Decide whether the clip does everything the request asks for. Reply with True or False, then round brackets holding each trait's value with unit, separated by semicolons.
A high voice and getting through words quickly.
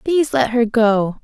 False (240 Hz; 195 wpm)